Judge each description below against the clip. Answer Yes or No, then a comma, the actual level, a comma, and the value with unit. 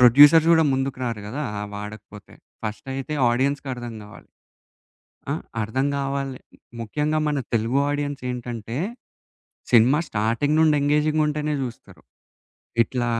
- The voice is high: No, low, 135 Hz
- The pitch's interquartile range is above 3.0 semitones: Yes, average, 4.0 semitones